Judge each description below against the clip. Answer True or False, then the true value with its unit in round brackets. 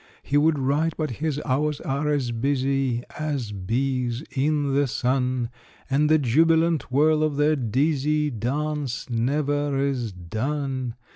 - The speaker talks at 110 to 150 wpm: True (135 wpm)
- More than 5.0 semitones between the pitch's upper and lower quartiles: False (3.0 semitones)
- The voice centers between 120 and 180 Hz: True (140 Hz)